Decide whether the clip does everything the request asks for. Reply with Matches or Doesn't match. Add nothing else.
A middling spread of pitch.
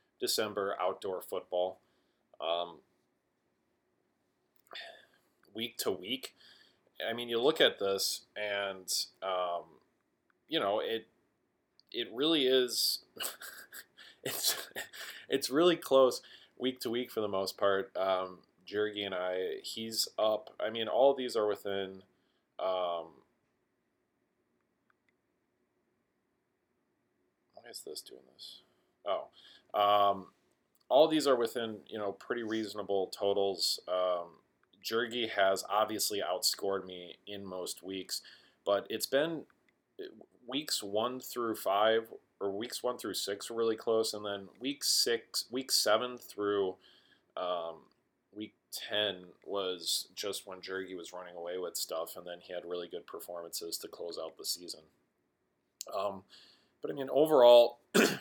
Matches